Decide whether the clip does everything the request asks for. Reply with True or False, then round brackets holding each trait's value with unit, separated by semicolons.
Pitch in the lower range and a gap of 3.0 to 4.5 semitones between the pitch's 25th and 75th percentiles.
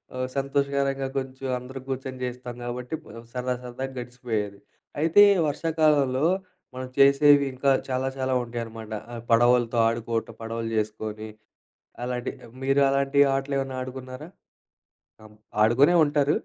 False (130 Hz; 2.4 semitones)